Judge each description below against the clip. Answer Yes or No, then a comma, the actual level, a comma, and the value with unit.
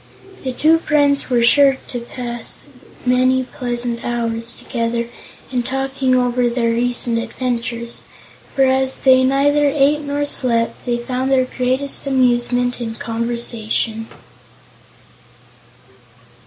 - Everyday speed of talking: No, slow, 115 wpm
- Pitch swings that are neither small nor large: No, narrow, 2.0 semitones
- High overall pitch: Yes, very high, 250 Hz